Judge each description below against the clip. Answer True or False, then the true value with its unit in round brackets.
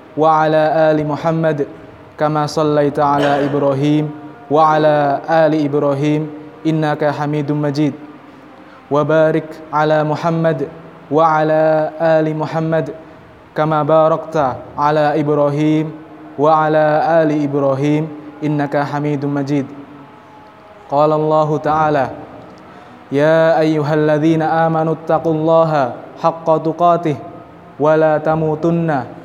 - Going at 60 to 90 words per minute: True (85 wpm)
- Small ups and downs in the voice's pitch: True (1.2 semitones)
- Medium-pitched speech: True (155 Hz)